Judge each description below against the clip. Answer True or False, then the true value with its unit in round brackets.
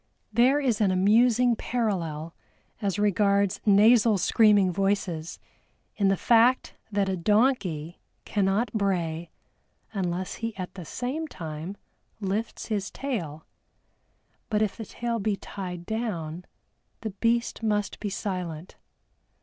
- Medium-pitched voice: False (200 Hz)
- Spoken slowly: True (120 wpm)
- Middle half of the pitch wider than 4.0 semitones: False (3.7 semitones)